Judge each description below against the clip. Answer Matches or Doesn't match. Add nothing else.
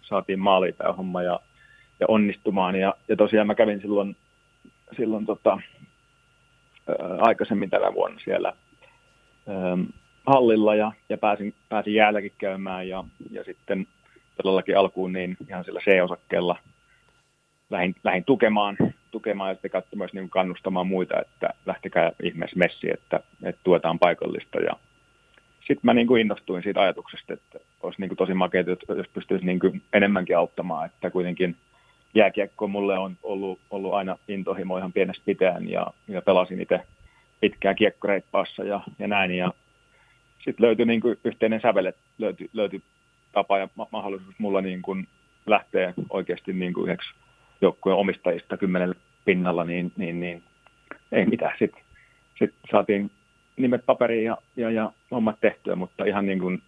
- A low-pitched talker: Matches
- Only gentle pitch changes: Matches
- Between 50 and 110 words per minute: Doesn't match